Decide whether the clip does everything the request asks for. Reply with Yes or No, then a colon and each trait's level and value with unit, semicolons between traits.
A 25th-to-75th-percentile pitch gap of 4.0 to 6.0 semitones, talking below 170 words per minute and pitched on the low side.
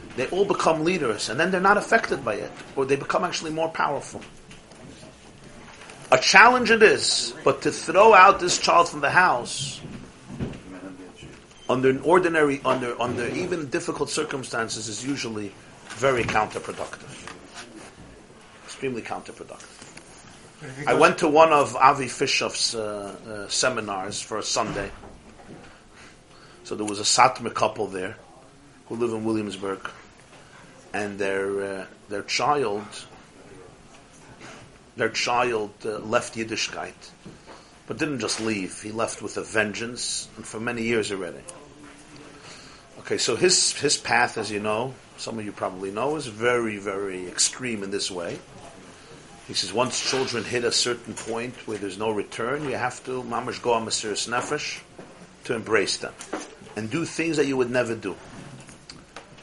Yes: wide, 5.6 semitones; average, 140 wpm; low, 120 Hz